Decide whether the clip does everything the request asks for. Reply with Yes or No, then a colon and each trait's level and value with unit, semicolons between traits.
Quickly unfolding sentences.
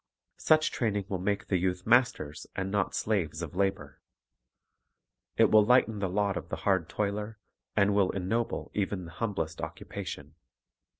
No: average, 155 wpm